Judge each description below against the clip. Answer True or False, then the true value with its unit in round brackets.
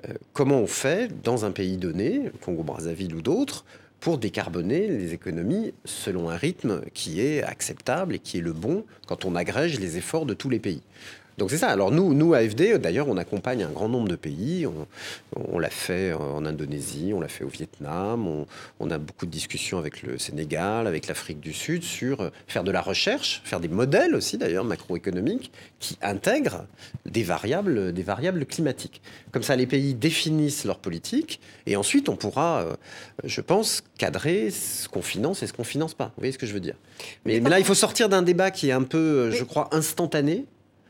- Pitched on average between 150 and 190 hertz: False (125 Hz)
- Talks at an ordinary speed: True (200 wpm)